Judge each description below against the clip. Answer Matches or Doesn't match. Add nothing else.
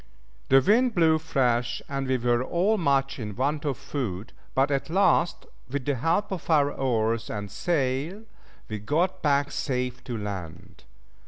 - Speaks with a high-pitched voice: Doesn't match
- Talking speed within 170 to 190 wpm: Doesn't match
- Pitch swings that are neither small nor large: Matches